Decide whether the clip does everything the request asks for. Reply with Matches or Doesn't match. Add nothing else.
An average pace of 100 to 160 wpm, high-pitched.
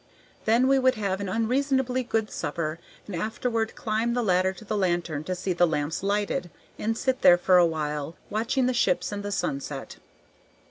Doesn't match